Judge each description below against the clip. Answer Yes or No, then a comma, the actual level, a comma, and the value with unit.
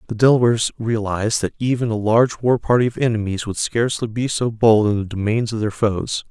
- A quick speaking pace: Yes, fast, 210 wpm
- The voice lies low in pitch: Yes, low, 110 Hz